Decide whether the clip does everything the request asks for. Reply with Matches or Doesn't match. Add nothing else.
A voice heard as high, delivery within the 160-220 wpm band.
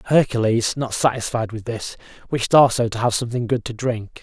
Doesn't match